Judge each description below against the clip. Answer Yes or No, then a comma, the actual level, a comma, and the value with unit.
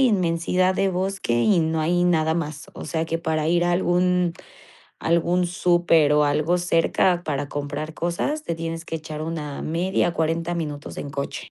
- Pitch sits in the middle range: Yes, medium, 165 Hz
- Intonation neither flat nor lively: No, narrow, 2.2 semitones